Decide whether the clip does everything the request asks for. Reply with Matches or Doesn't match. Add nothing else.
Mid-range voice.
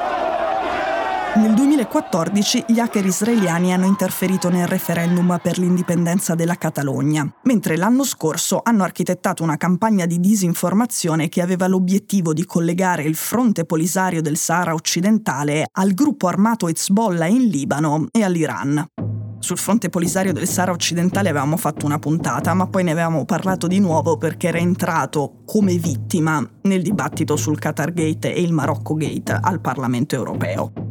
Matches